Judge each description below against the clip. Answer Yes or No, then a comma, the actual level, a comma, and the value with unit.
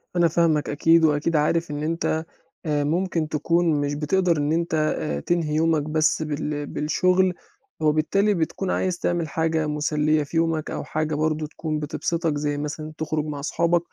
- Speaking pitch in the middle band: Yes, medium, 155 Hz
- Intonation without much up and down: Yes, narrow, 1.9 semitones